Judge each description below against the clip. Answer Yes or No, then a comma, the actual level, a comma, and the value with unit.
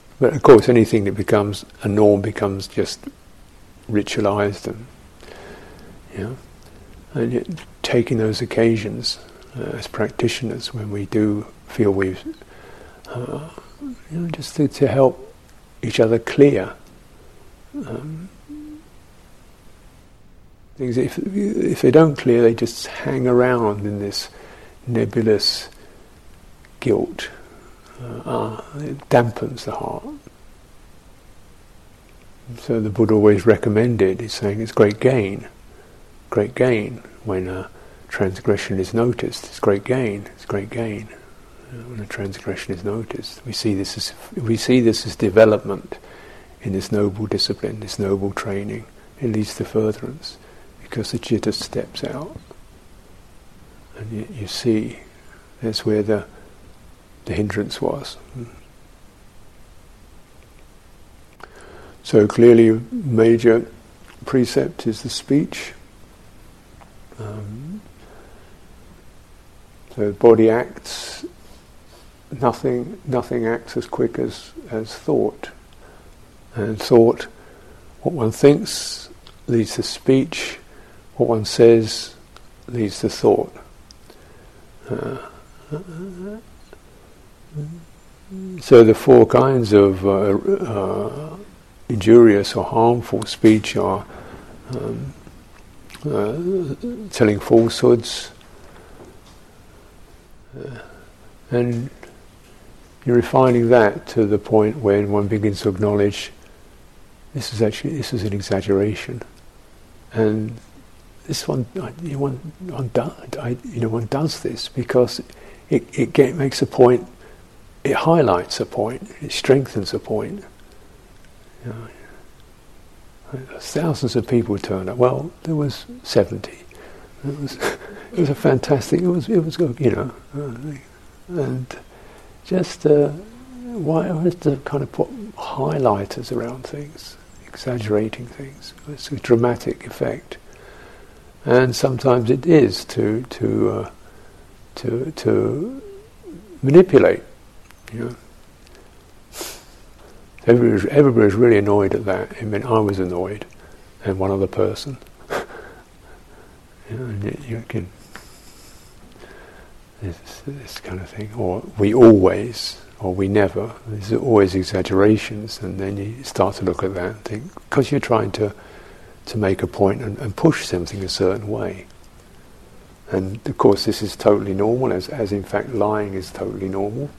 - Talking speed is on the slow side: Yes, slow, 120 wpm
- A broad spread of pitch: No, average, 4.0 semitones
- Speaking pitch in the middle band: No, low, 115 Hz